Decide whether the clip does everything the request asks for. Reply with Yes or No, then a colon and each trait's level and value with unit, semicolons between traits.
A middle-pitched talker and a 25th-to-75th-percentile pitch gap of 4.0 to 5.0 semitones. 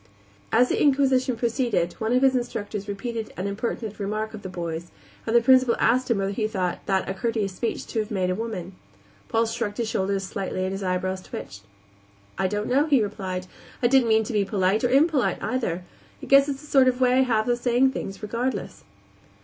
No: high, 220 Hz; average, 4.4 semitones